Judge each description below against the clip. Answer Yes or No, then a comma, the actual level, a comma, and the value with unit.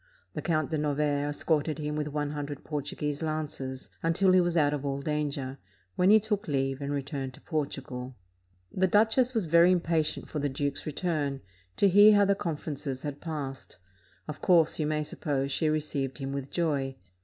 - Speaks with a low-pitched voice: No, medium, 150 Hz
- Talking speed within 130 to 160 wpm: No, average, 180 wpm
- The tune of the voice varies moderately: Yes, average, 3.0 semitones